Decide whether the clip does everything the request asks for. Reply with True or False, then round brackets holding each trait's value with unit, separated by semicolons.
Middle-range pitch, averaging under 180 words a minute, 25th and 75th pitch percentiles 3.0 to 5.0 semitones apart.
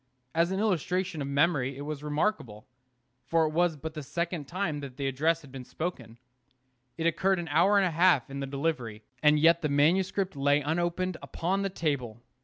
False (160 Hz; 195 wpm; 3.9 semitones)